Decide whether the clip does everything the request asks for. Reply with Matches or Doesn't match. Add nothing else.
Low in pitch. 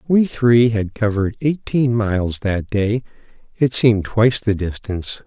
Matches